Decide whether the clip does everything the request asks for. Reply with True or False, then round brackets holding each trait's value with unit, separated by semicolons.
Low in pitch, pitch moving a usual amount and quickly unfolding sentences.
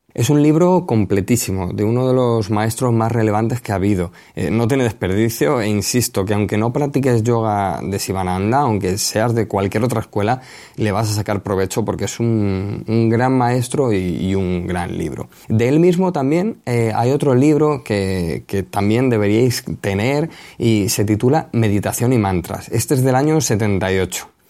False (110 Hz; 4.0 semitones; 180 wpm)